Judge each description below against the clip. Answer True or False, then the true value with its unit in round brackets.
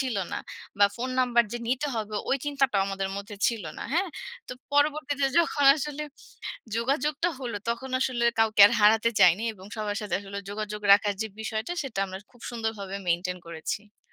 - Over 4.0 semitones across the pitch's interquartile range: True (4.6 semitones)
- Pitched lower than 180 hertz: False (225 Hz)